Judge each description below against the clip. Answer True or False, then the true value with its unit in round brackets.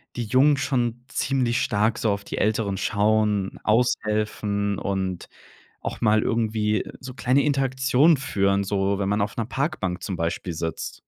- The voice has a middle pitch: False (110 Hz)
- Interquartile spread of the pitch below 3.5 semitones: False (3.8 semitones)